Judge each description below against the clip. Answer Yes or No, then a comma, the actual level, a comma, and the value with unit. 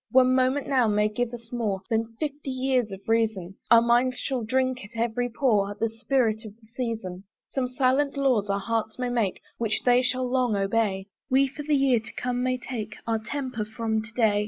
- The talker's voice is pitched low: No, high, 235 Hz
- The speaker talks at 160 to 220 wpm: Yes, fast, 205 wpm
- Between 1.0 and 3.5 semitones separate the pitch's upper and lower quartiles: Yes, average, 2.8 semitones